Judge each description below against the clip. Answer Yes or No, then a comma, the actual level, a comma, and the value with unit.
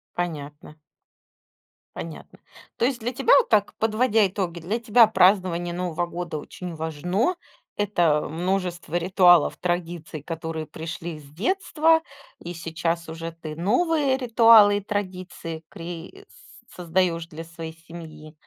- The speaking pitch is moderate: Yes, medium, 175 Hz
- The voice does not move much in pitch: No, average, 4.0 semitones